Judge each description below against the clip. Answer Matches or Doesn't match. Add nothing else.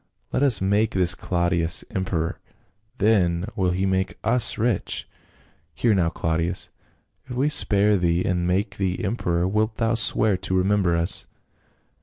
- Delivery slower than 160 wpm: Matches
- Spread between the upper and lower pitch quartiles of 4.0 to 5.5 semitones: Doesn't match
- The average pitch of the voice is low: Matches